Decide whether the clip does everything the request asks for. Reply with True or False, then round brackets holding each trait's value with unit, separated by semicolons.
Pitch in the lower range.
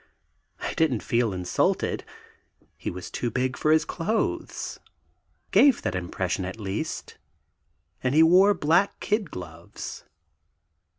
True (130 Hz)